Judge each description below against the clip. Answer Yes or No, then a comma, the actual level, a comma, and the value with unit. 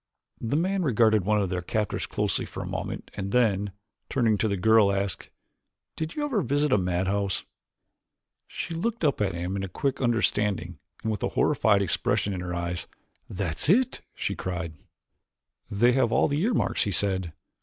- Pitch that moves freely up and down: Yes, wide, 5.9 semitones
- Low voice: Yes, low, 105 Hz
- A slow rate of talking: No, average, 175 wpm